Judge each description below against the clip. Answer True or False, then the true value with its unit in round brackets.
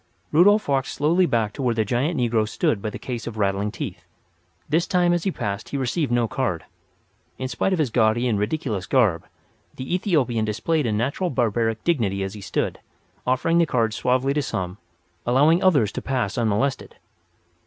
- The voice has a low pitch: True (125 Hz)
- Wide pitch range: True (5.7 semitones)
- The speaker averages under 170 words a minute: False (185 wpm)